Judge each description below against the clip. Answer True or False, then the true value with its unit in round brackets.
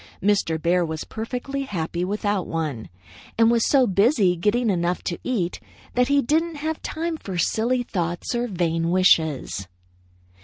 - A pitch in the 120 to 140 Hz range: False (200 Hz)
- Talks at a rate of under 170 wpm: True (150 wpm)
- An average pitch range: False (6.3 semitones)